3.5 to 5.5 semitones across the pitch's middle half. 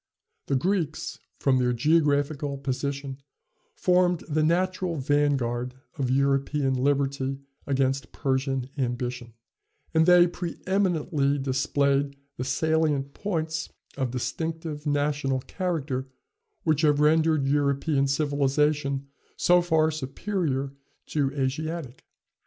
No: average, 2.9 semitones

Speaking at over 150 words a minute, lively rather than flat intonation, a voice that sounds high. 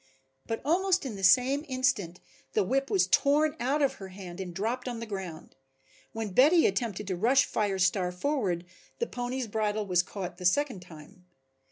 Yes: average, 180 wpm; wide, 6.4 semitones; high, 220 Hz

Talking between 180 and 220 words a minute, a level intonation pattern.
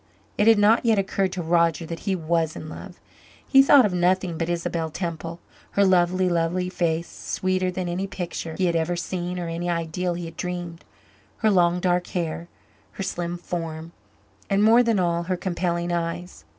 Yes: average, 185 wpm; narrow, 1.8 semitones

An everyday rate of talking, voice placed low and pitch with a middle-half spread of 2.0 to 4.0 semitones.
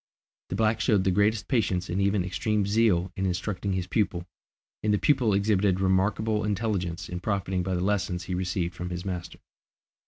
Yes: average, 180 wpm; very low, 95 Hz; average, 2.7 semitones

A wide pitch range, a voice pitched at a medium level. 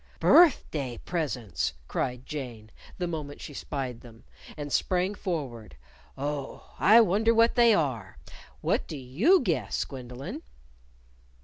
Yes: wide, 6.7 semitones; medium, 145 Hz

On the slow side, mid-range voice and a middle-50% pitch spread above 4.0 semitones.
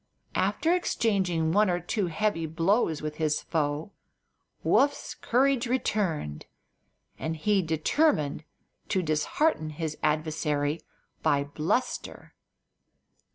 Yes: slow, 100 wpm; medium, 165 Hz; wide, 5.6 semitones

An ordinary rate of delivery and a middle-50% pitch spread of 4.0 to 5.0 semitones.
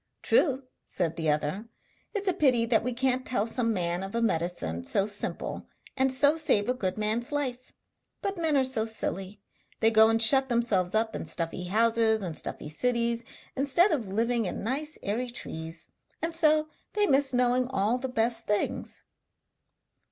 Yes: average, 175 wpm; average, 4.6 semitones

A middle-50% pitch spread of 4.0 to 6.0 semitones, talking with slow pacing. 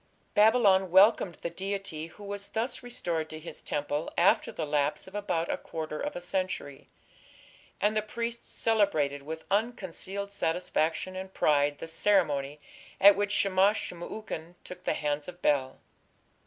No: average, 4.4 semitones; average, 155 wpm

